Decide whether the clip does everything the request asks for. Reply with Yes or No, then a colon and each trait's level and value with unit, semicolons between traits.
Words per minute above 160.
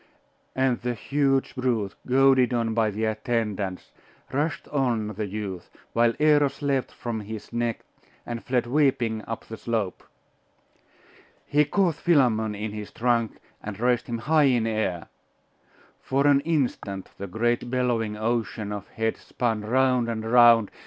No: average, 145 wpm